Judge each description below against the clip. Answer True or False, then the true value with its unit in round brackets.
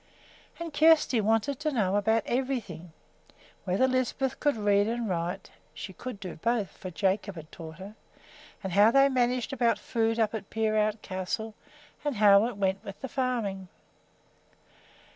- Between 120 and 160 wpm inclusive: True (155 wpm)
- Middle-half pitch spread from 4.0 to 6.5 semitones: True (4.4 semitones)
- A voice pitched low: False (220 Hz)